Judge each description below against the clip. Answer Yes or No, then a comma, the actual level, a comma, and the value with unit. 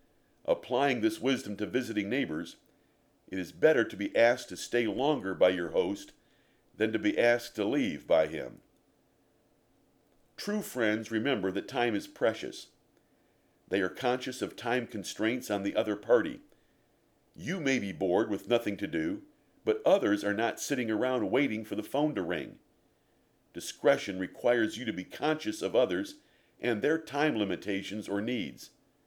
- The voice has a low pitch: Yes, low, 120 Hz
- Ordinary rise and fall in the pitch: No, wide, 6.7 semitones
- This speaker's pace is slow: No, average, 160 wpm